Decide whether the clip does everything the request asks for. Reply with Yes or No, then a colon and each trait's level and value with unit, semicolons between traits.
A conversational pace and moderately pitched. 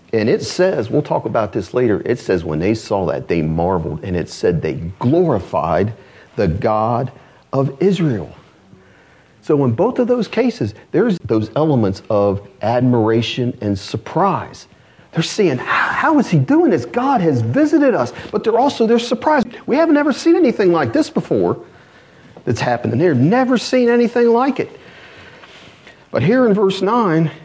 Yes: average, 170 wpm; medium, 165 Hz